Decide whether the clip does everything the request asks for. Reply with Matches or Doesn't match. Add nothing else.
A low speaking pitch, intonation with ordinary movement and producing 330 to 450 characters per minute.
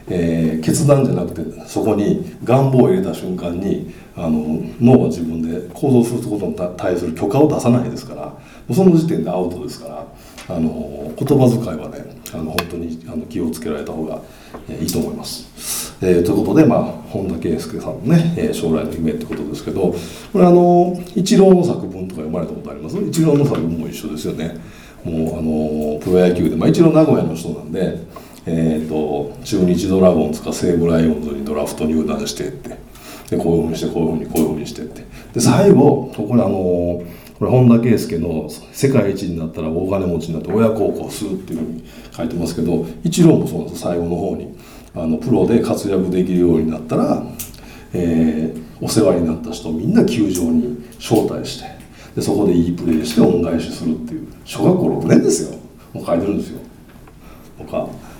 Doesn't match